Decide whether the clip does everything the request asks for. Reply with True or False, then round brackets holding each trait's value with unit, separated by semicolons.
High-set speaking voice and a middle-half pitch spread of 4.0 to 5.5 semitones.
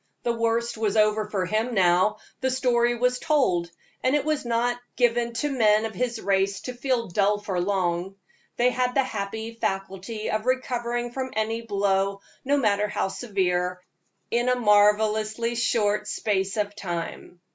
False (220 Hz; 3.4 semitones)